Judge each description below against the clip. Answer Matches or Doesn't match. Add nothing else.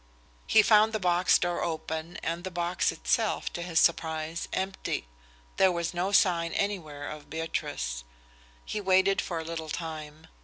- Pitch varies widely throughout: Doesn't match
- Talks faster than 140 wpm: Matches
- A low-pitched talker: Doesn't match